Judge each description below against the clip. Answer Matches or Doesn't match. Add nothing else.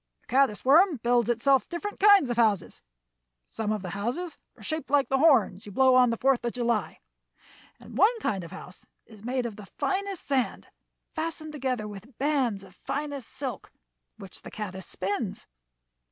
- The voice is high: Matches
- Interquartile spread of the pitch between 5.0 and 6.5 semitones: Matches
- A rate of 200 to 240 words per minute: Doesn't match